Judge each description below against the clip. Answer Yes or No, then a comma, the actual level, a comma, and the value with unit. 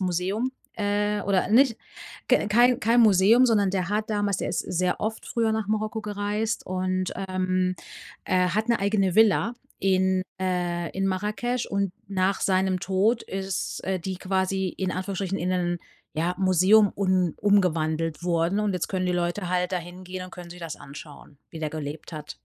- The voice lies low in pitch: No, high, 190 Hz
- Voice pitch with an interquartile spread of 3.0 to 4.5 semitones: No, narrow, 2.4 semitones